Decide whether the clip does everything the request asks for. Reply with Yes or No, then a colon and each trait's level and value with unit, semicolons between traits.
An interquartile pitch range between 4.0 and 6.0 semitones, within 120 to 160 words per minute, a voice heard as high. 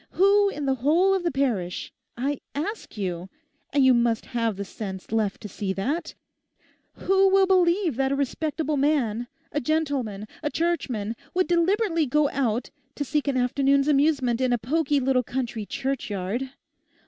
Yes: average, 5.3 semitones; average, 150 wpm; very high, 275 Hz